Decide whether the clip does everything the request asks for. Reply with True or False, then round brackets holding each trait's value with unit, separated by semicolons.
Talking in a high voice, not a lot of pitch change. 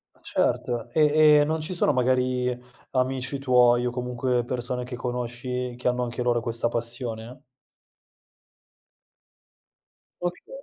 False (125 Hz; 1.1 semitones)